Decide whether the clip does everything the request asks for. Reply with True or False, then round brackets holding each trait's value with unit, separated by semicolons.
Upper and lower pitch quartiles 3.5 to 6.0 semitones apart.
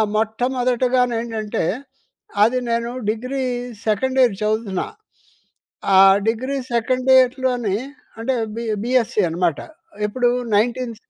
False (2.7 semitones)